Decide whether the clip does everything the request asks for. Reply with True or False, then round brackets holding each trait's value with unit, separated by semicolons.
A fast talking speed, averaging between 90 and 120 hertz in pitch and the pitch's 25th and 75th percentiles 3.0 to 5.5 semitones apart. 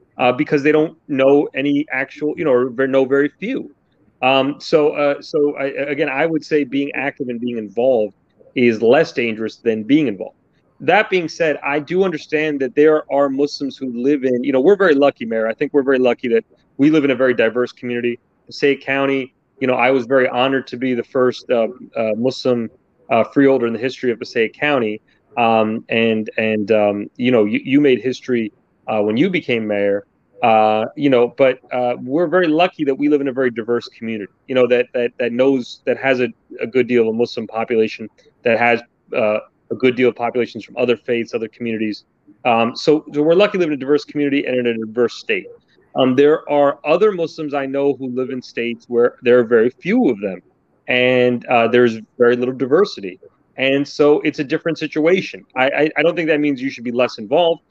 False (215 wpm; 130 Hz; 3.4 semitones)